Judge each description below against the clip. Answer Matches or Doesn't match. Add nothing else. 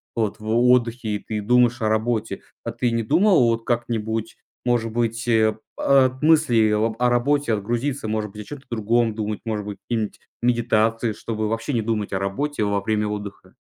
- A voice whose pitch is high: Doesn't match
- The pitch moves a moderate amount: Doesn't match